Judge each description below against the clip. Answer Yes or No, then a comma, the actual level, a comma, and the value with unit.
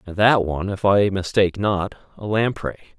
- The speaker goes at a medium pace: Yes, average, 180 wpm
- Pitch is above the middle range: No, low, 100 Hz